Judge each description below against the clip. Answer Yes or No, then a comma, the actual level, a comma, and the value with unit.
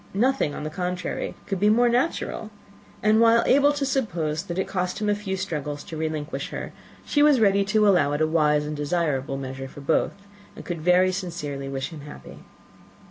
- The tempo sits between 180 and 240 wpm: Yes, average, 195 wpm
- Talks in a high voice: No, medium, 180 Hz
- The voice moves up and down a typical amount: No, wide, 6.0 semitones